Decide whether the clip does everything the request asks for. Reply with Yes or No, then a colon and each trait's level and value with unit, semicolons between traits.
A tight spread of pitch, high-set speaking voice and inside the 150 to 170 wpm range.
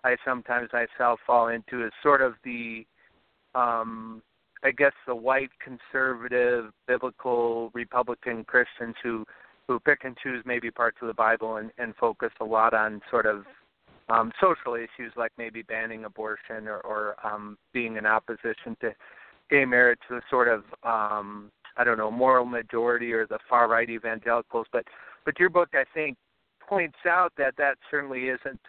No: narrow, 2.3 semitones; low, 120 Hz; average, 165 wpm